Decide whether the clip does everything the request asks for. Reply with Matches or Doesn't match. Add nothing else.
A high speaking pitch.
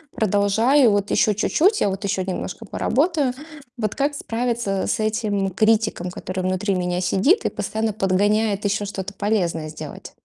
Matches